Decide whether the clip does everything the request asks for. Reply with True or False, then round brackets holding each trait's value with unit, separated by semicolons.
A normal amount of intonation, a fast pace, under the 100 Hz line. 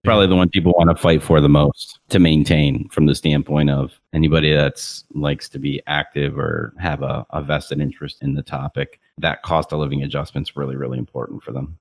False (2.2 semitones; 210 wpm; 75 Hz)